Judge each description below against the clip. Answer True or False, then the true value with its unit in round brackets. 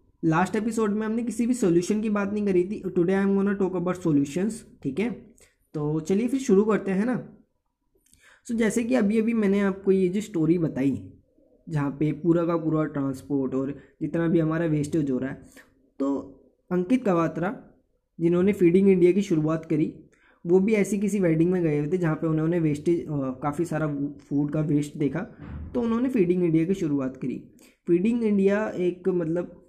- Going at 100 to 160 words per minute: False (190 wpm)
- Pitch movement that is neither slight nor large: True (4.7 semitones)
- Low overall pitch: False (175 Hz)